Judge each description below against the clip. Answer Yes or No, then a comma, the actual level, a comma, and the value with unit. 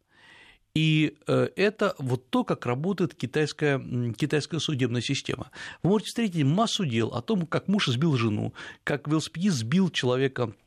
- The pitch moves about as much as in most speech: No, wide, 6.1 semitones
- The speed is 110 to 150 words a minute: Yes, average, 140 wpm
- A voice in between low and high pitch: Yes, medium, 150 Hz